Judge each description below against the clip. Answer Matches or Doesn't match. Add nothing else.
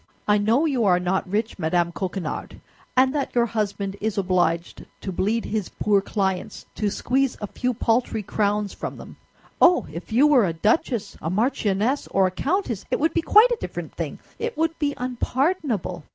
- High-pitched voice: Matches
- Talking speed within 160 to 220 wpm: Matches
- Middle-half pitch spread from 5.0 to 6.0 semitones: Matches